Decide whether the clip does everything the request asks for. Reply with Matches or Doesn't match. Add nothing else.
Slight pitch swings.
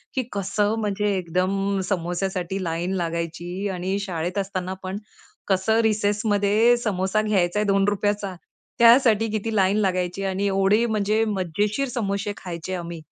Matches